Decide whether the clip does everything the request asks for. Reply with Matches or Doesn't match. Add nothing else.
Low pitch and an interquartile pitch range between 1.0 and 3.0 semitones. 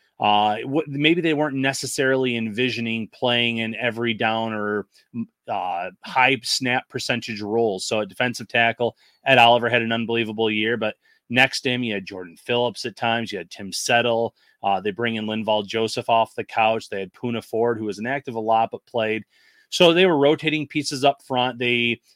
Matches